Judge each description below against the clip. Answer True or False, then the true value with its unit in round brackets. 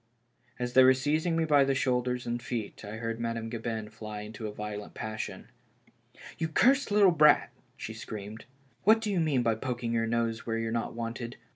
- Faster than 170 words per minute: True (190 wpm)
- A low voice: True (120 Hz)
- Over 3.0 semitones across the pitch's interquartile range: True (3.8 semitones)